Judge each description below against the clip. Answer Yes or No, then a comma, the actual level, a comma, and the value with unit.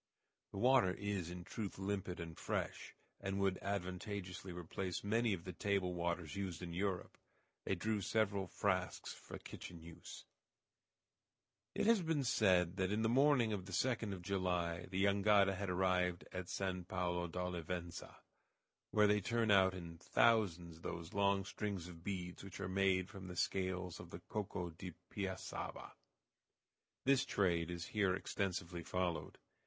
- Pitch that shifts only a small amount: Yes, narrow, 2.3 semitones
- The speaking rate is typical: Yes, average, 155 wpm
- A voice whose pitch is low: Yes, very low, 95 Hz